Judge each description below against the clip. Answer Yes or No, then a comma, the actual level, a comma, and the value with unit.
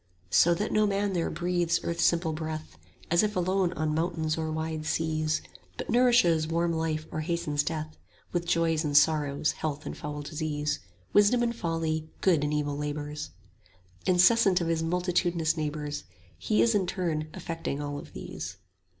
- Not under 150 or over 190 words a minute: Yes, average, 165 wpm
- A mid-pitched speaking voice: Yes, medium, 160 Hz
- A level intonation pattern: Yes, narrow, 2.3 semitones